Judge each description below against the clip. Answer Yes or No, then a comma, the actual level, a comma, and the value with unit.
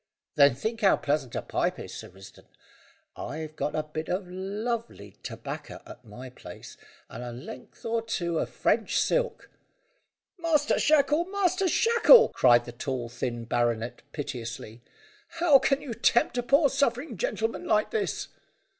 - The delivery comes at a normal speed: Yes, average, 150 wpm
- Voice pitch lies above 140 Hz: Yes, high, 190 Hz